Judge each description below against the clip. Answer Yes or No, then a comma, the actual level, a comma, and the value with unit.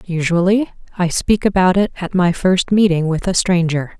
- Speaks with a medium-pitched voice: Yes, medium, 180 Hz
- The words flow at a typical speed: Yes, average, 180 wpm